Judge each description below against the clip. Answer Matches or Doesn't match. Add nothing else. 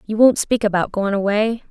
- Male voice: Doesn't match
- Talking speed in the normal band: Doesn't match